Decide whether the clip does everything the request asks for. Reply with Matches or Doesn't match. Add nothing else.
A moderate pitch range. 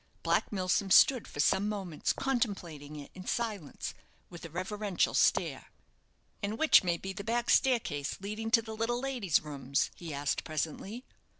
Doesn't match